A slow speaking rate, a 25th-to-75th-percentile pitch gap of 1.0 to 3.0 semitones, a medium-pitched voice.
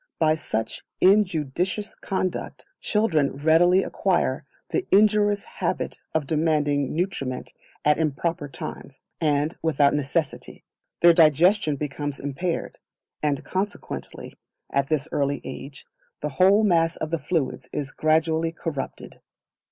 No: slow, 115 wpm; average, 3.7 semitones; medium, 160 Hz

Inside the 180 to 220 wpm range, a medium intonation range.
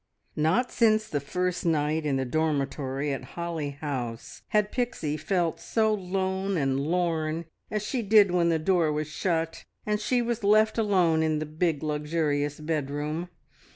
No: average, 155 wpm; average, 4.5 semitones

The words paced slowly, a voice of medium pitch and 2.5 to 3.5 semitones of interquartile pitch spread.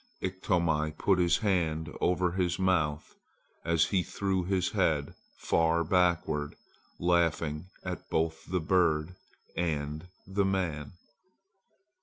No: slow, 105 wpm; very low, 85 Hz; average, 2.8 semitones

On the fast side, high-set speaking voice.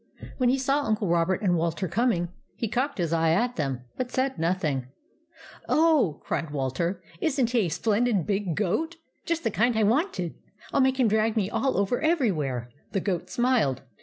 Yes: fast, 210 wpm; high, 210 Hz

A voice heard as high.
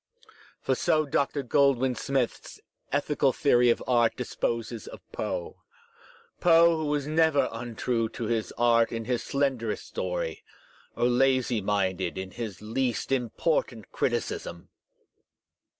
No: low, 125 Hz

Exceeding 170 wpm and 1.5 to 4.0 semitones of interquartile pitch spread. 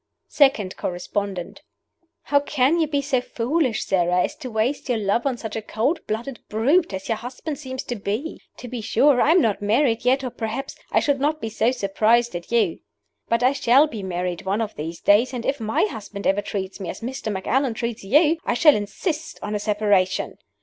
No: fast, 205 wpm; average, 4.9 semitones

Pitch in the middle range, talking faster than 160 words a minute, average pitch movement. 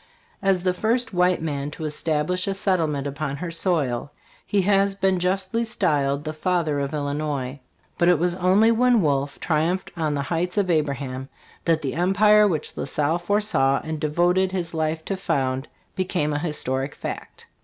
Yes: medium, 165 Hz; average, 170 wpm; average, 4.3 semitones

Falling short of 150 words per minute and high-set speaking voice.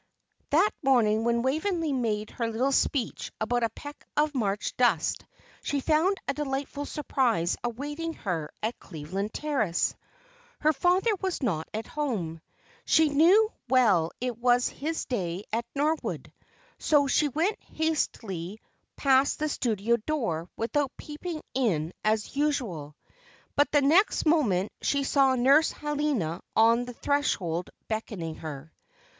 Yes: slow, 135 wpm; very high, 255 Hz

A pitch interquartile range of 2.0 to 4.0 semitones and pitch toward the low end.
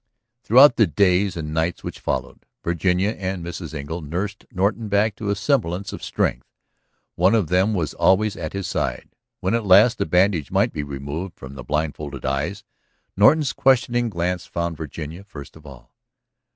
No: average, 4.7 semitones; very low, 90 Hz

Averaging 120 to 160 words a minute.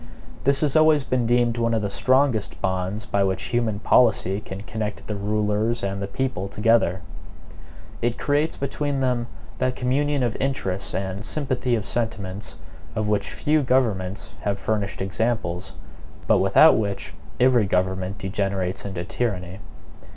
Yes: average, 145 wpm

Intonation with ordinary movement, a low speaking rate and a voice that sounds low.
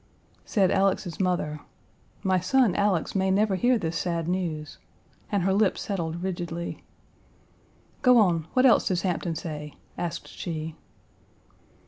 No: average, 3.0 semitones; slow, 130 wpm; medium, 180 Hz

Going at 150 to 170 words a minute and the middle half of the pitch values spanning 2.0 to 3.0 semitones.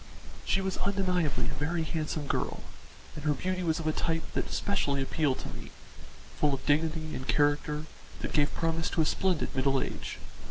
No: average, 185 wpm; narrow, 2.4 semitones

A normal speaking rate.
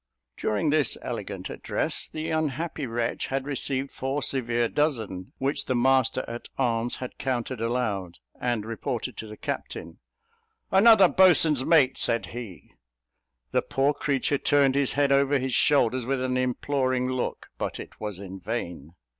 Yes: average, 150 wpm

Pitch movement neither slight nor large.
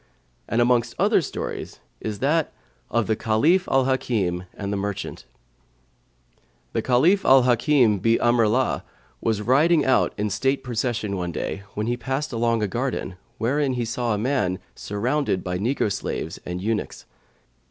Yes: average, 4.1 semitones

